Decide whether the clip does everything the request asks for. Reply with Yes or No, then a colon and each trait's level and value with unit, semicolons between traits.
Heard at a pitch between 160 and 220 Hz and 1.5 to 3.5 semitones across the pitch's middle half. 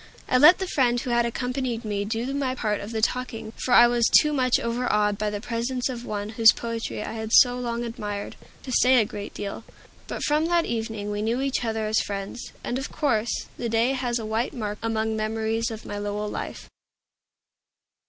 No: high, 230 Hz; narrow, 2.6 semitones